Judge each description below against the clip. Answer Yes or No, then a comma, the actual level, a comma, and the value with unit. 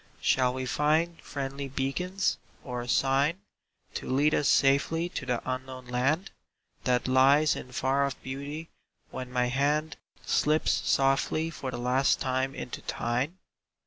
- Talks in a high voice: No, low, 135 Hz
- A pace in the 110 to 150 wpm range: Yes, average, 145 wpm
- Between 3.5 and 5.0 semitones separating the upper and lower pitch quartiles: No, average, 2.8 semitones